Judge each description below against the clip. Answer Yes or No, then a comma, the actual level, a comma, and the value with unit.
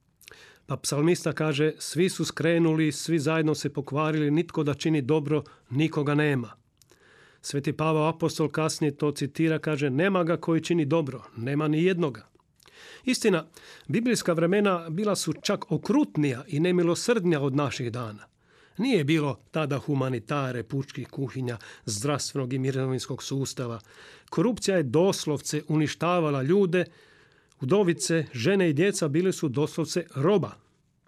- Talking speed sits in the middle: Yes, average, 125 wpm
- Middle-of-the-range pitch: Yes, medium, 155 Hz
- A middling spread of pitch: Yes, average, 3.1 semitones